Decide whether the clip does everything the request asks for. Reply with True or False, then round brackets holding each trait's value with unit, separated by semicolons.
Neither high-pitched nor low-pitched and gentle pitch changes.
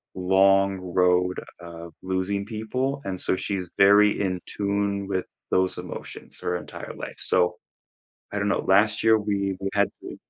False (95 Hz; 1.8 semitones)